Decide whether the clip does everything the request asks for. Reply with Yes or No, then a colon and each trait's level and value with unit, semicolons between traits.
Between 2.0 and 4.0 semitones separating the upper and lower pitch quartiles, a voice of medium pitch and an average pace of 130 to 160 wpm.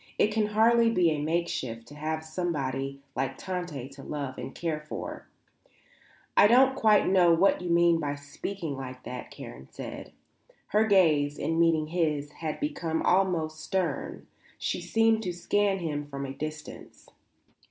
No: average, 4.6 semitones; medium, 165 Hz; average, 155 wpm